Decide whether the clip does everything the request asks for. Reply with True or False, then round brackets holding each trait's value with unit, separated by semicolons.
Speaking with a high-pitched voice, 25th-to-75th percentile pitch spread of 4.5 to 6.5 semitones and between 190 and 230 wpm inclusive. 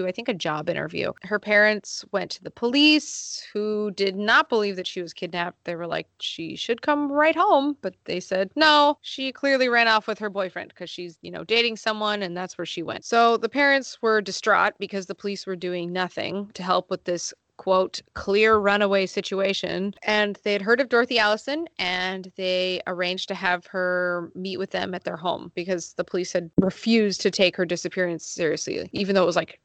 False (195 Hz; 3.4 semitones; 205 wpm)